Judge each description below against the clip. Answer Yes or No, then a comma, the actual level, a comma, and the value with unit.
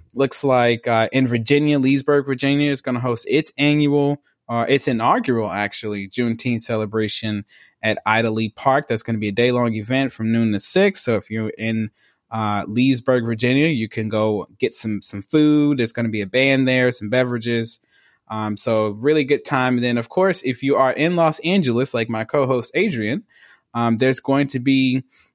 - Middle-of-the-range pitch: No, low, 125 Hz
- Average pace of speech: Yes, average, 195 wpm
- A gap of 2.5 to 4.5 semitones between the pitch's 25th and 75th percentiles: Yes, average, 3.6 semitones